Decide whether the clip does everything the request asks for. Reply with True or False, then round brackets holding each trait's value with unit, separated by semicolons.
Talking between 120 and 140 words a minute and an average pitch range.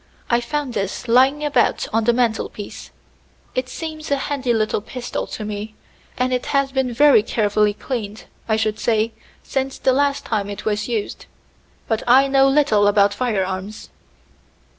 False (160 wpm; 4.1 semitones)